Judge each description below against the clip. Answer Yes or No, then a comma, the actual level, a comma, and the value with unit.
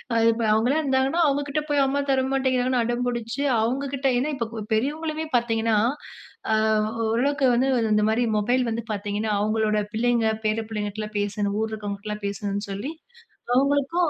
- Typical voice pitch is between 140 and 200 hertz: No, high, 235 Hz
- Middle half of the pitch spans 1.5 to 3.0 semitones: No, average, 4.1 semitones